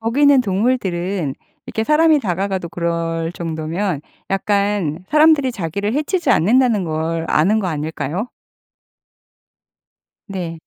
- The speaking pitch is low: No, high, 190 Hz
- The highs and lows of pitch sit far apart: Yes, wide, 5.8 semitones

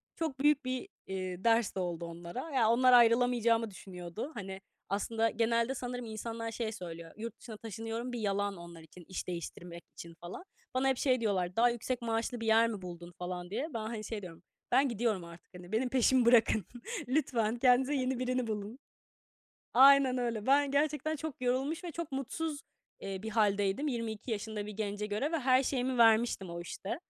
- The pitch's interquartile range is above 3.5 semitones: Yes, average, 4.4 semitones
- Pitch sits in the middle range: No, high, 230 Hz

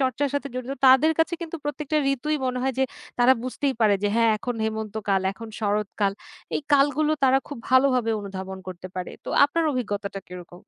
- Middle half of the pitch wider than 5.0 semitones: Yes, wide, 5.4 semitones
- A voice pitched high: Yes, very high, 250 Hz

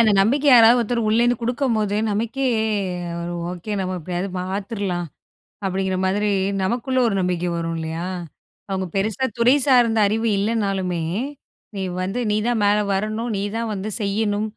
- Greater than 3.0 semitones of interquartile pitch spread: Yes, average, 3.6 semitones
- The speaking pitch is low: No, high, 210 Hz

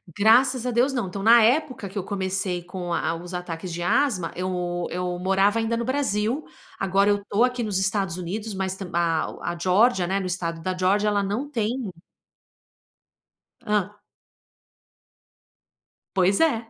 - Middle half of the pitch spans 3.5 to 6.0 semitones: Yes, average, 3.8 semitones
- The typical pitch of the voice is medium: No, high, 195 Hz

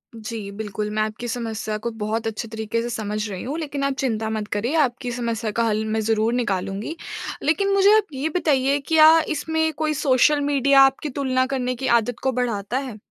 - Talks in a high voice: Yes, high, 245 Hz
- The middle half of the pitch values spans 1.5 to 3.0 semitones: No, average, 4.3 semitones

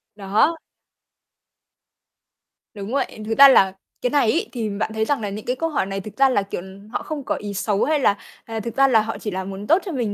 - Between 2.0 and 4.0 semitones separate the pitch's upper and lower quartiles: No, average, 5.1 semitones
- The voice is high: Yes, high, 220 Hz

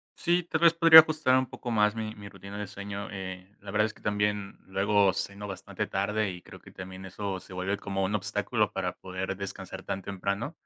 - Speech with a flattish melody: Yes, narrow, 1.7 semitones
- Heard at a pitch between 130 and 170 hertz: No, low, 100 Hz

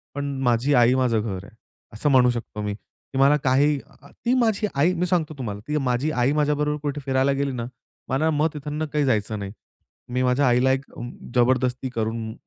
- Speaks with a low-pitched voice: Yes, low, 130 Hz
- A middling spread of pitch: Yes, average, 3.4 semitones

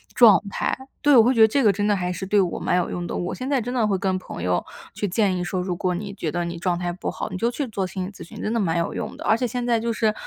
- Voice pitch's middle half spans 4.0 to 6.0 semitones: Yes, average, 4.3 semitones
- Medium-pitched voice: No, high, 200 Hz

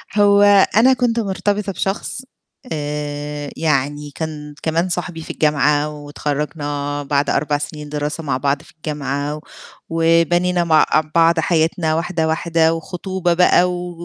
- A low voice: No, medium, 160 Hz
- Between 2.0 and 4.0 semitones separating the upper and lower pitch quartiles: Yes, average, 3.1 semitones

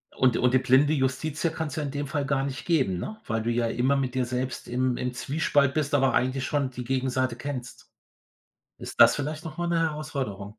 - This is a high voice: No, low, 135 Hz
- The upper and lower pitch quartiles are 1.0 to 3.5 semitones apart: Yes, narrow, 2.6 semitones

